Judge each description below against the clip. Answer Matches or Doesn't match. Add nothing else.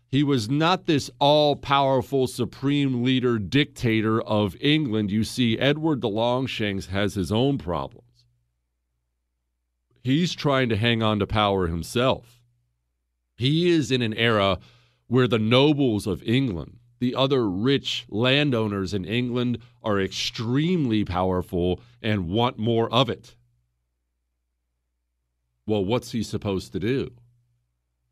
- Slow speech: Matches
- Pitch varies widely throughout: Matches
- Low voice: Matches